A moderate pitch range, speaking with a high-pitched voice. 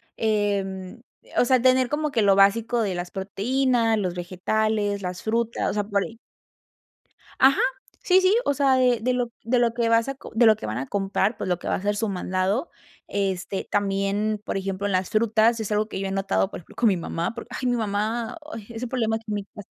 Yes: average, 3.2 semitones; high, 215 Hz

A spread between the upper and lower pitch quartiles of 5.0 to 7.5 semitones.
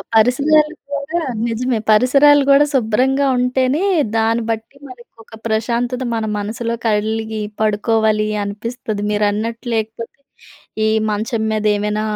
No: average, 2.8 semitones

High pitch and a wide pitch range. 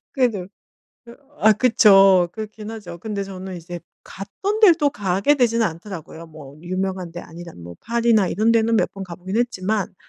No: high, 195 Hz; average, 4.3 semitones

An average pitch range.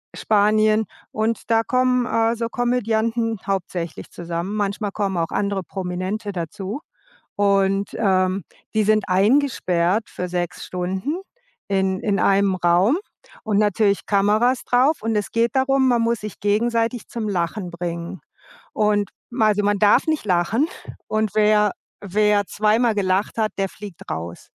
Yes: average, 3.0 semitones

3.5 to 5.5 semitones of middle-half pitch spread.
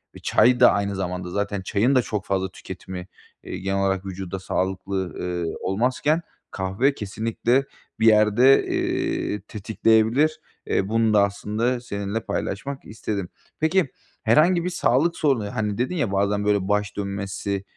Yes: average, 4.0 semitones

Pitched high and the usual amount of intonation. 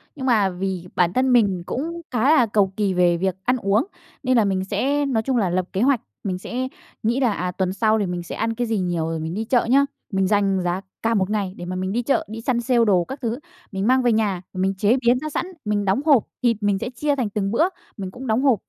Yes: high, 215 Hz; average, 4.6 semitones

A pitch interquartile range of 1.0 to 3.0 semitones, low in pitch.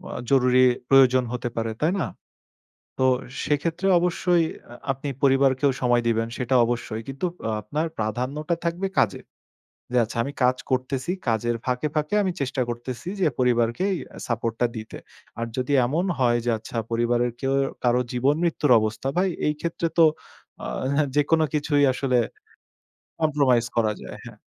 No: average, 3.9 semitones; low, 130 Hz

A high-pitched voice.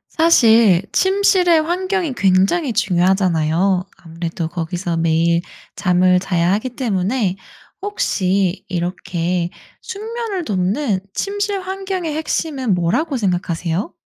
Yes: high, 195 Hz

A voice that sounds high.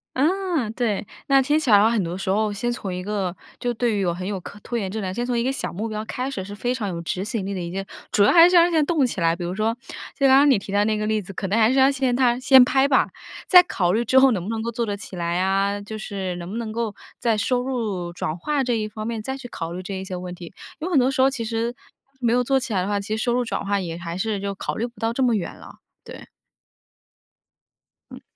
Yes: high, 220 Hz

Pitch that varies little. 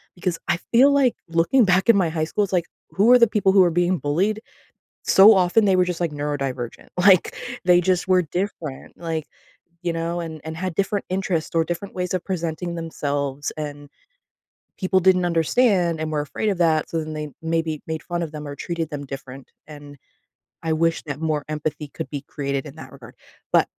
No: average, 3.5 semitones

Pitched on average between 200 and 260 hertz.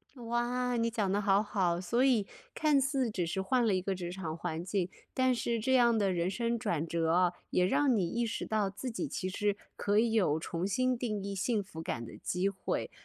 Yes: high, 205 Hz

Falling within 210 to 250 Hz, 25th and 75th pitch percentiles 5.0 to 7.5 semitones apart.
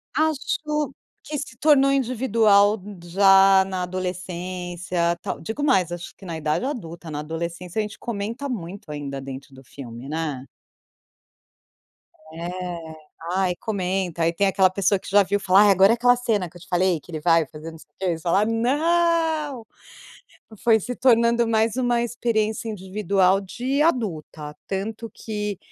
No: high, 195 Hz; average, 5.3 semitones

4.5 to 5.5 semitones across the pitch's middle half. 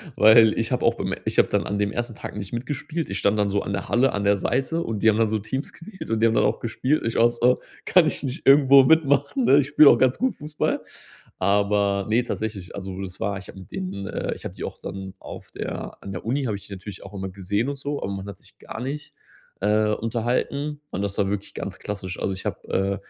Yes: average, 5.0 semitones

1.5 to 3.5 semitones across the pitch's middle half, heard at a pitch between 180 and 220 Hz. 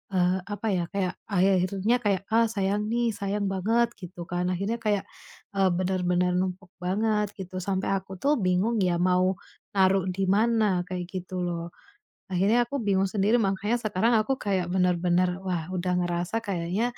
Yes: narrow, 2.5 semitones; high, 190 Hz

